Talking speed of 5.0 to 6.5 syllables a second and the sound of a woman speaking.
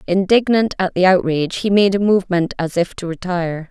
Yes: 5.7 syllables/s; female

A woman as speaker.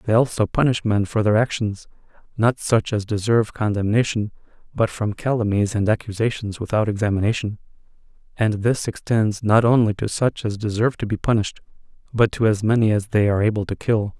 No: male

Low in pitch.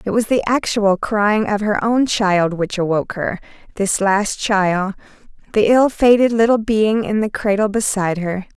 No: high, 205 Hz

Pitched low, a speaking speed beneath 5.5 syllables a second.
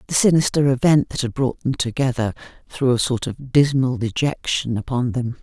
Yes: low, 130 Hz; 5.1 syllables/s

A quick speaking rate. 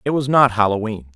Yes: fast, 210 wpm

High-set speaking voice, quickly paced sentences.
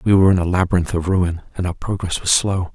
No: very low, 90 Hz; fast, 265 wpm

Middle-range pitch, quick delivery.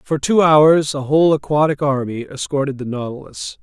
No: medium, 145 Hz; average, 165 wpm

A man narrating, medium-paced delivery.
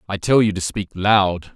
No: male; fast, 230 wpm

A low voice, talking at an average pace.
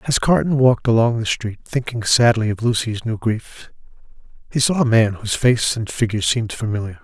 Yes: low, 115 Hz; average, 190 wpm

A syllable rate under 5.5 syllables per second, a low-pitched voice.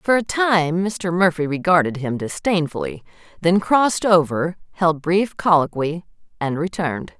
No: 4.5 syllables/s; medium, 175 Hz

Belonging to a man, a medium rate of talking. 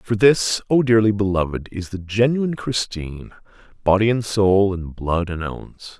Yes: male; average, 160 wpm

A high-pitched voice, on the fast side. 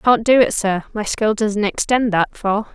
Yes: high, 215 Hz; fast, 220 wpm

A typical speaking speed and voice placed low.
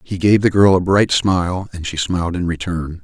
No: fast, 235 wpm; very low, 90 Hz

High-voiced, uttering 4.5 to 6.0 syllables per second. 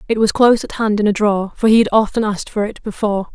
No: high, 210 Hz; 7.2 syllables/s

